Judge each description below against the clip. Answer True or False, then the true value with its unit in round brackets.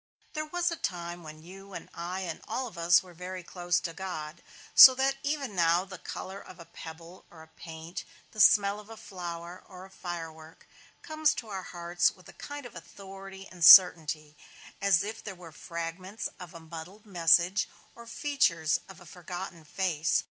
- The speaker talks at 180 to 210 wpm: True (190 wpm)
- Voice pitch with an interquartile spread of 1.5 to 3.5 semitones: True (2.9 semitones)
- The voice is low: False (180 Hz)